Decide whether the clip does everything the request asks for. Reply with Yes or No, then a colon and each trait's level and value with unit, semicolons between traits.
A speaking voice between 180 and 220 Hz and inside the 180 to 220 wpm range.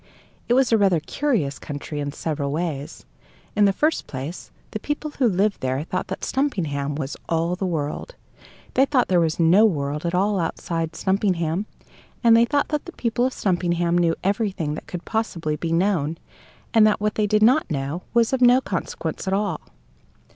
Yes: medium, 185 Hz; average, 185 wpm